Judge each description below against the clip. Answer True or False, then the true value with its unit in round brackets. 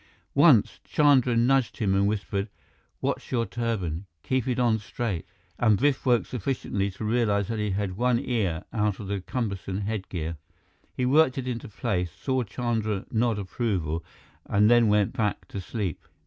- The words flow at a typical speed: True (160 wpm)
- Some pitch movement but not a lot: True (3.6 semitones)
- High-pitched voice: False (110 Hz)